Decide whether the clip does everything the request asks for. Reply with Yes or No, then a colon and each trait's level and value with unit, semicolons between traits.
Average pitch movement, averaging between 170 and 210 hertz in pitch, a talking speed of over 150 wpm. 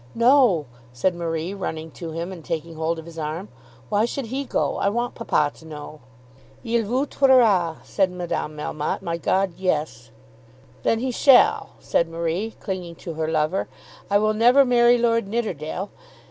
No: wide, 6.2 semitones; medium, 185 Hz; average, 165 wpm